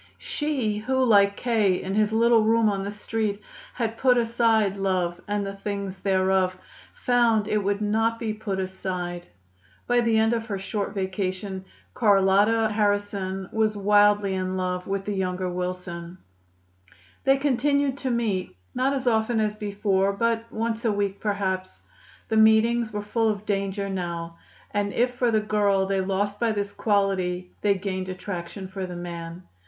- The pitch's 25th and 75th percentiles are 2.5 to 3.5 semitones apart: Yes, average, 2.8 semitones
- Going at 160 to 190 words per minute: Yes, average, 165 wpm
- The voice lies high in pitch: Yes, high, 205 Hz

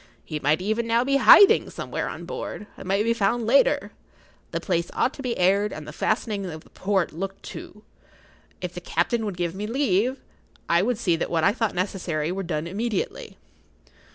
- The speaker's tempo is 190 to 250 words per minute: Yes, average, 195 wpm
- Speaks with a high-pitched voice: Yes, high, 200 Hz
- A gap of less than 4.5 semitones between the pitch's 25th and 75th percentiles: No, average, 4.9 semitones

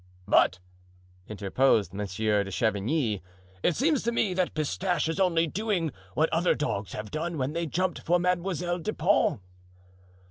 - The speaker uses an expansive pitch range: Yes, wide, 8.7 semitones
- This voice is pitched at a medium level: Yes, medium, 160 Hz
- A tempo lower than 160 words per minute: Yes, average, 150 wpm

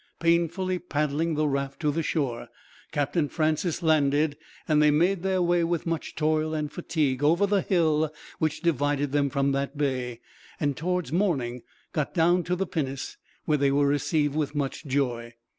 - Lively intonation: No, average, 3.0 semitones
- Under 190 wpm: Yes, average, 170 wpm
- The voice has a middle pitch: Yes, medium, 150 Hz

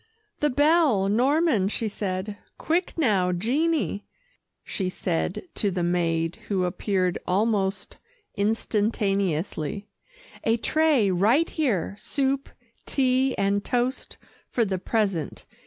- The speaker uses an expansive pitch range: Yes, wide, 5.7 semitones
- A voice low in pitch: No, high, 205 Hz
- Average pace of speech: No, slow, 105 wpm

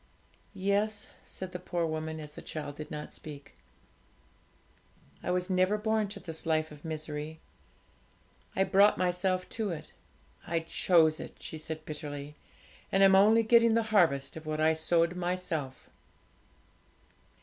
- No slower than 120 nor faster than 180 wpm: Yes, average, 145 wpm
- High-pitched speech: No, medium, 170 Hz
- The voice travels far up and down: No, average, 3.7 semitones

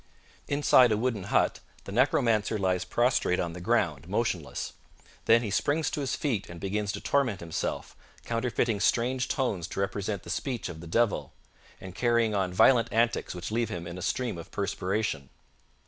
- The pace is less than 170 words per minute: No, average, 175 wpm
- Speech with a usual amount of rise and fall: Yes, average, 4.6 semitones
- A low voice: Yes, low, 105 Hz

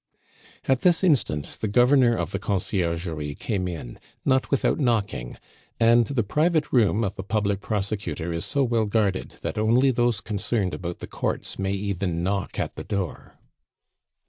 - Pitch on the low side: Yes, low, 105 Hz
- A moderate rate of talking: Yes, average, 160 wpm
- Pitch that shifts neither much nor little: Yes, average, 4.4 semitones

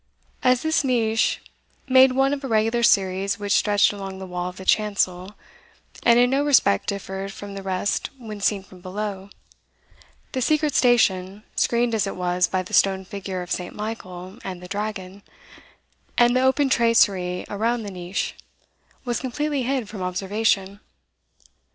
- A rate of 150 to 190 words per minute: Yes, average, 160 wpm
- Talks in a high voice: Yes, high, 205 Hz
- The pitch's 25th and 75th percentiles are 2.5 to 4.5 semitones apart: Yes, average, 4.2 semitones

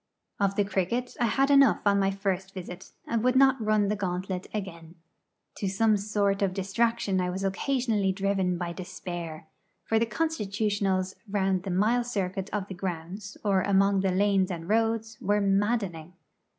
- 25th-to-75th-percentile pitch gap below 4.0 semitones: Yes, narrow, 2.4 semitones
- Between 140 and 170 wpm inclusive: Yes, average, 165 wpm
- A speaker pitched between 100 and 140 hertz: No, high, 195 Hz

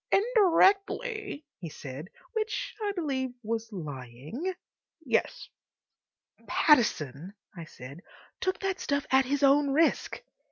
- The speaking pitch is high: Yes, very high, 275 Hz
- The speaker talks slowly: Yes, slow, 110 wpm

